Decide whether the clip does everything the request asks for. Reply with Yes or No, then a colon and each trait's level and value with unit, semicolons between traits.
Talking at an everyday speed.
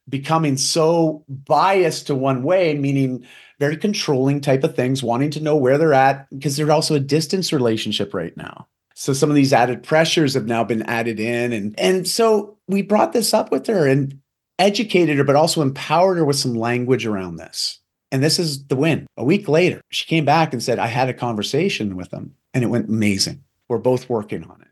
No: fast, 210 wpm